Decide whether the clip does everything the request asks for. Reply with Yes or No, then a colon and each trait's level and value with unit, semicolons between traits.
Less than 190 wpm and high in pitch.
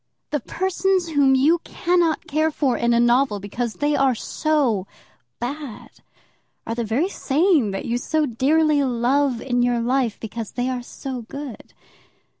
Yes: average, 155 wpm; very high, 265 Hz